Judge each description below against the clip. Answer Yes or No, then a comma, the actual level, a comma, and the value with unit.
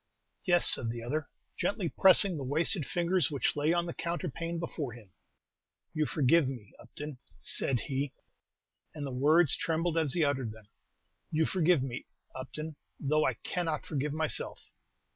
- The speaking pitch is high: No, medium, 150 Hz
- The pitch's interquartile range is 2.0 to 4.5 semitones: Yes, average, 4.1 semitones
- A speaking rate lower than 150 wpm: No, average, 155 wpm